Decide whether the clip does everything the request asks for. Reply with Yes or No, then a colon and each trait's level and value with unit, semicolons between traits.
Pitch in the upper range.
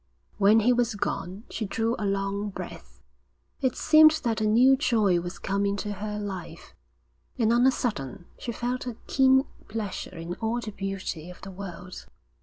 Yes: high, 210 Hz